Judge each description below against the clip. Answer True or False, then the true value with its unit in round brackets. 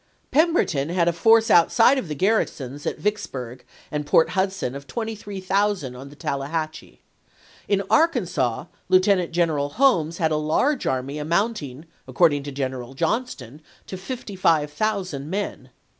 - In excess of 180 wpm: False (145 wpm)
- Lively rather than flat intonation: True (6.3 semitones)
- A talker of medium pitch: True (170 Hz)